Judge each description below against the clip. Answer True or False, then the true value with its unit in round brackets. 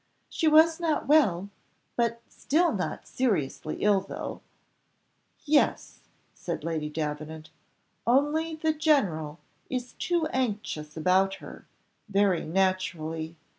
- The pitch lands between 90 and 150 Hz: False (200 Hz)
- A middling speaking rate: False (110 wpm)